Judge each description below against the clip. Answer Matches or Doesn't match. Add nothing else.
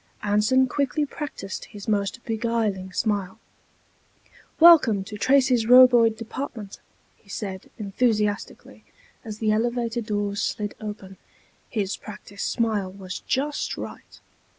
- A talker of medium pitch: Doesn't match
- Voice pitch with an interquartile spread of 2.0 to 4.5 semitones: Matches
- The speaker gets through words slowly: Matches